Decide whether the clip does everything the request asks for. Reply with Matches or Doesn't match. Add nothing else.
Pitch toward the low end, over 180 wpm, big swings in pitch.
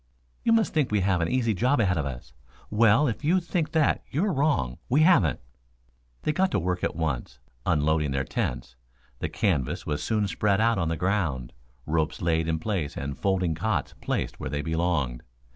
Matches